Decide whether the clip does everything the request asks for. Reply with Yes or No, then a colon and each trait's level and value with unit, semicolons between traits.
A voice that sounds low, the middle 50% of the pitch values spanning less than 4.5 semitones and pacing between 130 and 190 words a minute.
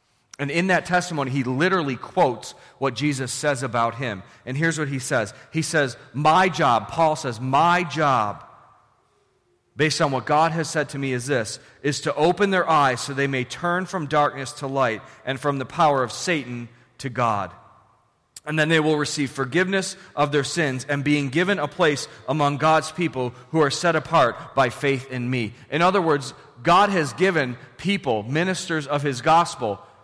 No: medium, 145 Hz; average, 3.8 semitones; average, 185 wpm